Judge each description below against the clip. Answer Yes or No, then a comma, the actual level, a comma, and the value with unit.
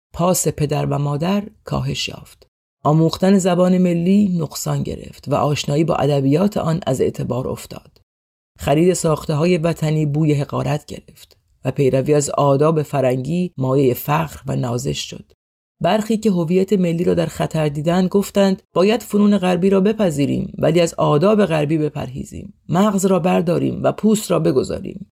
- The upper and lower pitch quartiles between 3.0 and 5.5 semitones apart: Yes, average, 4.5 semitones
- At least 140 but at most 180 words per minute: Yes, average, 150 wpm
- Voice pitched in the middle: Yes, medium, 160 Hz